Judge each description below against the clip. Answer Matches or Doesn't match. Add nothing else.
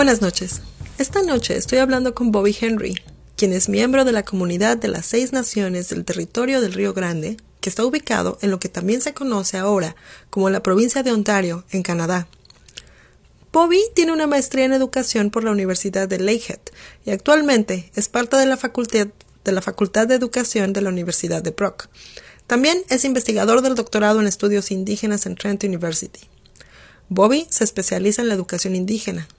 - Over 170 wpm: Matches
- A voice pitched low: Doesn't match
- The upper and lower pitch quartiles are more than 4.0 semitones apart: Matches